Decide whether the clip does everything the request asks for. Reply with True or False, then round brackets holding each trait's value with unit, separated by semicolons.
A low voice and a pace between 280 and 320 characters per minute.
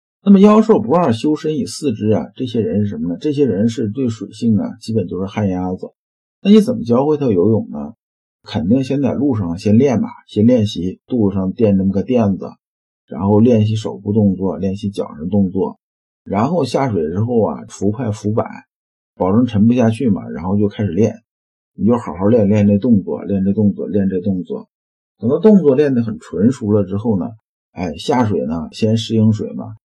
True (110 Hz; 285 characters per minute)